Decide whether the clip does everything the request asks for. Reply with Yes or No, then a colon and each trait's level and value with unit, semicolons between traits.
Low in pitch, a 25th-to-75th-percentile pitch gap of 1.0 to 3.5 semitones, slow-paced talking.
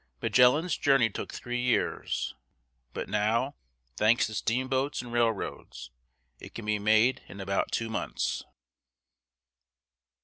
Yes: low, 115 Hz; average, 3.0 semitones; slow, 115 wpm